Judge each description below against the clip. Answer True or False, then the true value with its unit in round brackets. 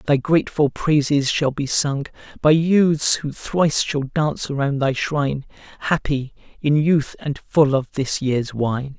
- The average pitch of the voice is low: False (145 Hz)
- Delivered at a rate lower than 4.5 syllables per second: True (4.1 syllables/s)